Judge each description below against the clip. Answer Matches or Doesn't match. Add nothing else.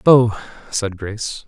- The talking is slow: Matches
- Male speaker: Matches